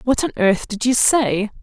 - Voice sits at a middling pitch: No, high, 230 Hz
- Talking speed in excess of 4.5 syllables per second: No, 4.4 syllables/s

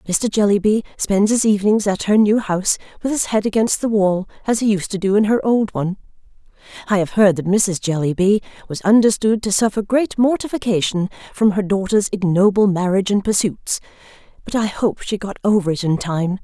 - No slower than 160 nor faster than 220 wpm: Yes, average, 190 wpm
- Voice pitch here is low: No, high, 200 Hz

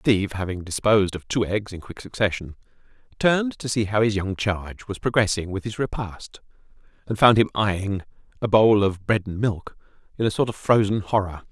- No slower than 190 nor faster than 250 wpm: Yes, average, 195 wpm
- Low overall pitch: Yes, low, 105 Hz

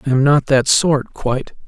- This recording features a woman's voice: No, male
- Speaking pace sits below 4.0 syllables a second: No, 4.8 syllables/s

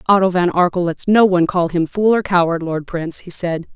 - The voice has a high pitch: No, medium, 180 Hz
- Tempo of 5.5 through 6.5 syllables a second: Yes, 5.7 syllables/s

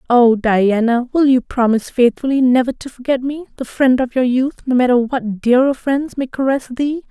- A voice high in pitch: Yes, very high, 255 Hz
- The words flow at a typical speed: Yes, average, 195 wpm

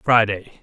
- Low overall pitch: Yes, low, 110 Hz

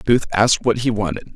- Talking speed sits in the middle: No, fast, 220 wpm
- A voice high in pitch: No, low, 110 Hz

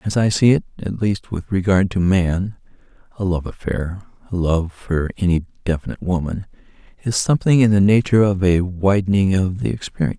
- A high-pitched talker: No, very low, 95 Hz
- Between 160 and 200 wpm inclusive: Yes, average, 170 wpm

